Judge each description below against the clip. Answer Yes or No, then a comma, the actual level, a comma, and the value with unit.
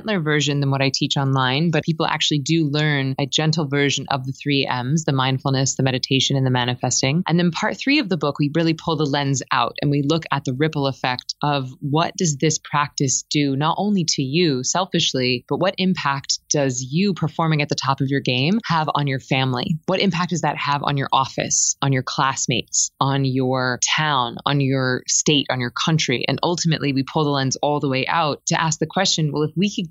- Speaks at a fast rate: Yes, fast, 220 wpm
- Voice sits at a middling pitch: Yes, medium, 145 Hz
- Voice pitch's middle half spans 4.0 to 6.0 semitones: No, average, 3.3 semitones